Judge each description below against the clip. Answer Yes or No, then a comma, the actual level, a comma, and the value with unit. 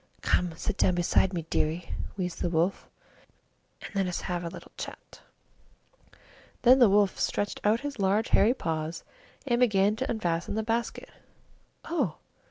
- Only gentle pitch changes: No, average, 4.5 semitones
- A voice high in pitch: Yes, high, 195 Hz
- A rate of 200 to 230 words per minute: No, average, 165 wpm